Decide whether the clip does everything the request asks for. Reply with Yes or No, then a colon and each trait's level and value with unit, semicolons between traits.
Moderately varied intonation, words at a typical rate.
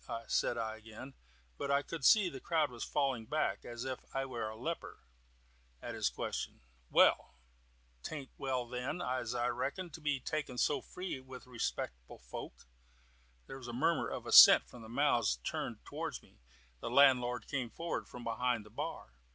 Yes: average, 3.1 semitones; average, 170 wpm